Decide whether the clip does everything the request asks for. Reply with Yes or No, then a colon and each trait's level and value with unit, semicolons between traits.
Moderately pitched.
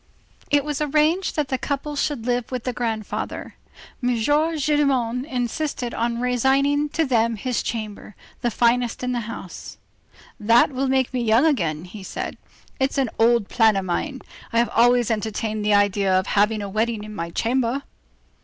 No: high, 240 Hz